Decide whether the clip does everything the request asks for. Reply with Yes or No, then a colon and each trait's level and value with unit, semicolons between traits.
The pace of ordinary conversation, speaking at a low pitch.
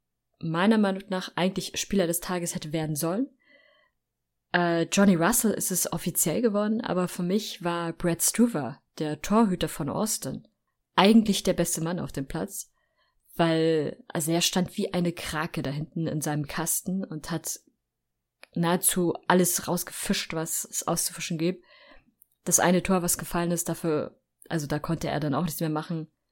No: average, 160 wpm; medium, 175 Hz